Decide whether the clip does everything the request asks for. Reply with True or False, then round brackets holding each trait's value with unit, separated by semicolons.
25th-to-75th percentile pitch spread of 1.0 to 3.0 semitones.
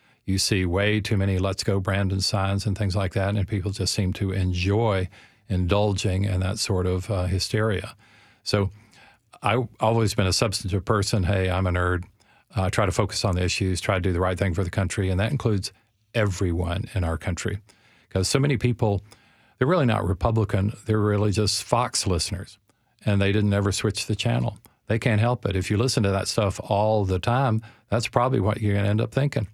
True (2.5 semitones)